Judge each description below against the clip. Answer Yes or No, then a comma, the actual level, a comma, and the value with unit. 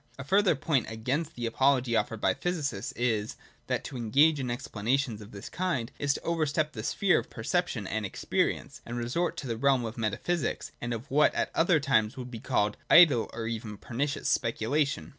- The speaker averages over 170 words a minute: Yes, average, 195 wpm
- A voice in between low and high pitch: No, low, 125 Hz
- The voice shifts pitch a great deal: No, average, 4.9 semitones